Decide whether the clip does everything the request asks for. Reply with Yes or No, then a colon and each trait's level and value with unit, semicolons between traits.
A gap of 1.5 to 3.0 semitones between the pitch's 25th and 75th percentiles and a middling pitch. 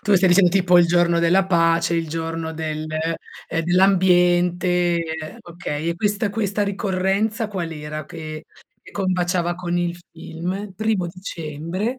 Yes: narrow, 2.5 semitones; medium, 175 Hz